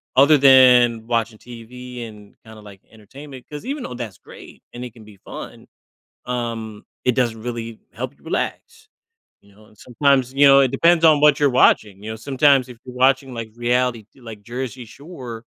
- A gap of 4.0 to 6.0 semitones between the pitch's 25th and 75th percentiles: No, average, 3.2 semitones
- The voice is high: No, low, 125 Hz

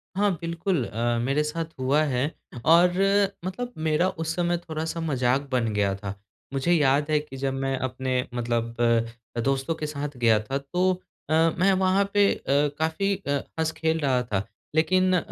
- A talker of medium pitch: Yes, medium, 150 Hz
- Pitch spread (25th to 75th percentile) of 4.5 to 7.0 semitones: Yes, average, 5.0 semitones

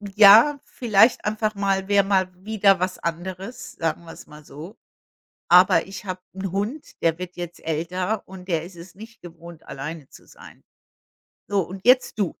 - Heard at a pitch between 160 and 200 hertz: Yes, high, 190 Hz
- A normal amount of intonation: Yes, average, 3.1 semitones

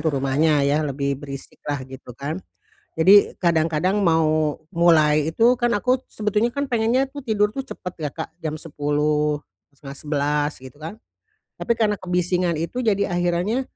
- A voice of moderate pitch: Yes, medium, 160 Hz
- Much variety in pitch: Yes, wide, 5.9 semitones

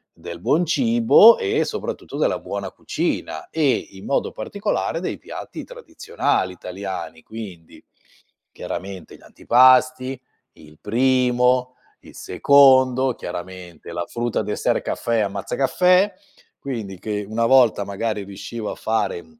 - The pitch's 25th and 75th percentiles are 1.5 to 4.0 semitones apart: No, wide, 5.5 semitones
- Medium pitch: No, low, 120 Hz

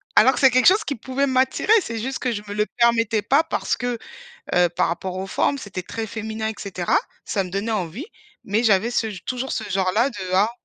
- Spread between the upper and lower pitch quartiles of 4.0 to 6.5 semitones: Yes, average, 4.5 semitones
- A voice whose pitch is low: No, high, 225 Hz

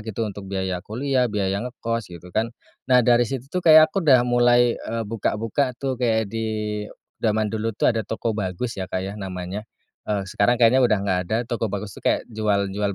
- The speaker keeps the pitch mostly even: No, average, 3.3 semitones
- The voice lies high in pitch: No, low, 110 Hz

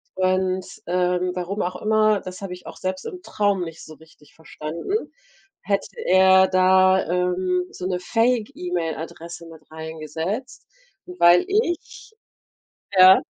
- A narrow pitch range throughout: Yes, narrow, 2.3 semitones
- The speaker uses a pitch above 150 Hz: Yes, medium, 185 Hz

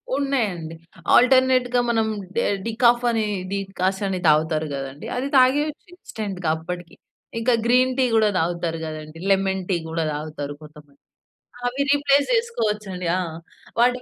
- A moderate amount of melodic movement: No, wide, 7.4 semitones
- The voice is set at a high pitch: Yes, high, 200 Hz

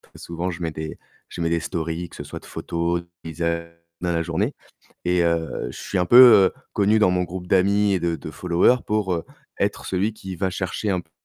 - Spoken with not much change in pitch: Yes, narrow, 2.3 semitones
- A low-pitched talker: Yes, very low, 90 Hz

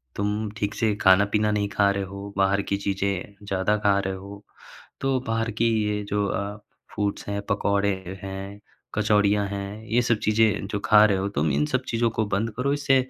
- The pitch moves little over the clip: Yes, narrow, 1.5 semitones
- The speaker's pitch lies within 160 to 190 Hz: No, low, 100 Hz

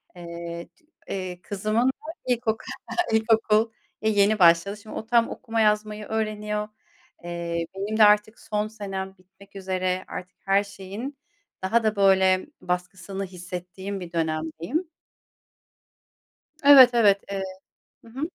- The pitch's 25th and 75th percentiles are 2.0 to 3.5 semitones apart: Yes, average, 2.9 semitones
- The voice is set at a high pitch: Yes, high, 200 Hz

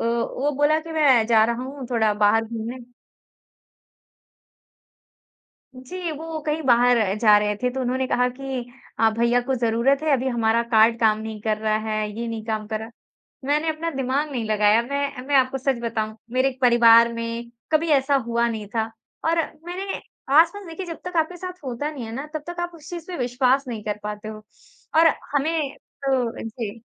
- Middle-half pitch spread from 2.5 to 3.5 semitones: No, average, 4.2 semitones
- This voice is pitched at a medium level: No, very high, 250 Hz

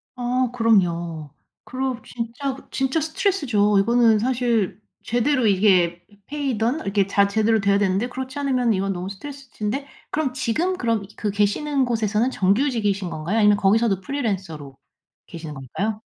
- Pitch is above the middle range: Yes, high, 220 Hz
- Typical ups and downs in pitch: Yes, average, 4.7 semitones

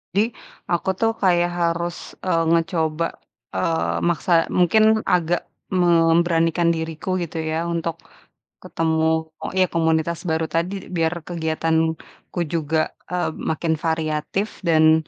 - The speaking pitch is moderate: Yes, medium, 165 Hz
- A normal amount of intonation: No, narrow, 1.4 semitones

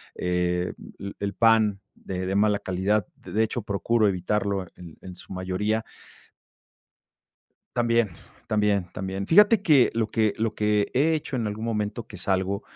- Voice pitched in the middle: No, low, 105 Hz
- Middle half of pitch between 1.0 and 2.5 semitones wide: No, average, 2.9 semitones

